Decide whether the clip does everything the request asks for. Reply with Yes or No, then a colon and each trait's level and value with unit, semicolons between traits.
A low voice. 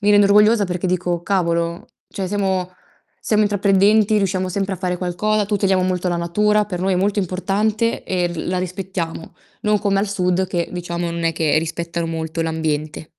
No: medium, 185 Hz